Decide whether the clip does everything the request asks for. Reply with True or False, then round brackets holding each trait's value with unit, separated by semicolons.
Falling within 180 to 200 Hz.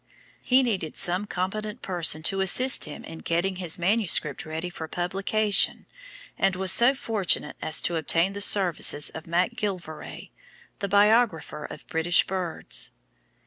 True (185 Hz)